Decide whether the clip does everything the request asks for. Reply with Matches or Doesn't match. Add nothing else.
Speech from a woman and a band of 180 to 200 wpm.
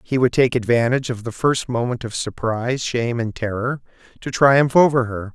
Doesn't match